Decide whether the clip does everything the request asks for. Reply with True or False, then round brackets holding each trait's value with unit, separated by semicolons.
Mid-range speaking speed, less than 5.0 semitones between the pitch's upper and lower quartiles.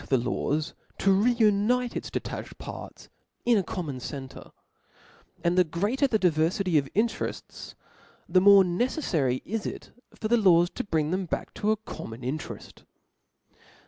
False (145 wpm; 5.6 semitones)